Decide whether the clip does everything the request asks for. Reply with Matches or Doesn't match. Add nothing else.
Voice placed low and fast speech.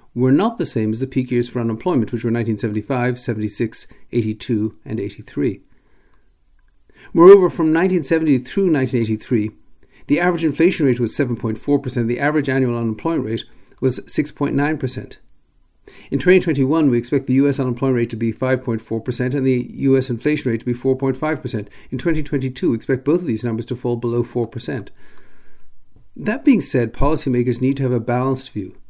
Doesn't match